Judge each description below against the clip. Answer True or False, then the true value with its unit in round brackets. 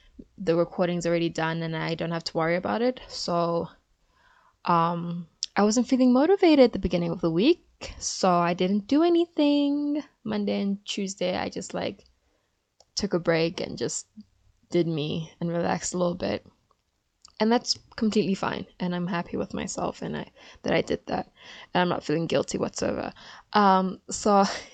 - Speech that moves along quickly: False (170 wpm)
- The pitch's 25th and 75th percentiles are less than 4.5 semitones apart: False (5.4 semitones)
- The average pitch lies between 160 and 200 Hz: True (185 Hz)